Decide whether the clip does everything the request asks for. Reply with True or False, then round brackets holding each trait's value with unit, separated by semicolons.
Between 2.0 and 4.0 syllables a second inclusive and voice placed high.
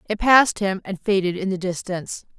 False (5.8 syllables/s; 195 Hz)